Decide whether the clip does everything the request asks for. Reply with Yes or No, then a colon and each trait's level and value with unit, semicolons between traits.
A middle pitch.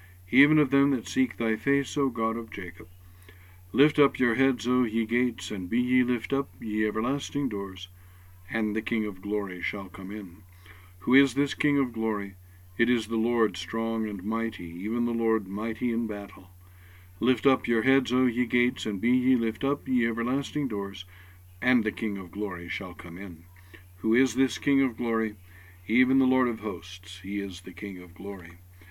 No: low, 110 Hz